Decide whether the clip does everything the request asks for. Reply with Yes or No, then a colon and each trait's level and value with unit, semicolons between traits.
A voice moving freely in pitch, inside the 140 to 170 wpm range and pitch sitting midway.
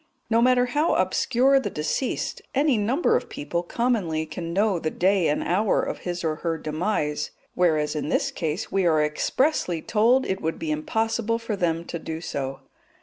No: wide, 6.4 semitones; average, 180 wpm; medium, 180 Hz